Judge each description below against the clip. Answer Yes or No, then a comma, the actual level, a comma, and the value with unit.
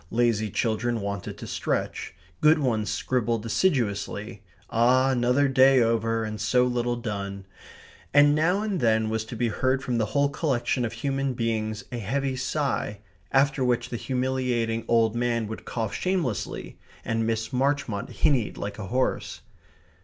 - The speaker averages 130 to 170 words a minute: Yes, average, 155 wpm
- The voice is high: No, low, 120 Hz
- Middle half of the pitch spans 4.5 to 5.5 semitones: No, average, 3.0 semitones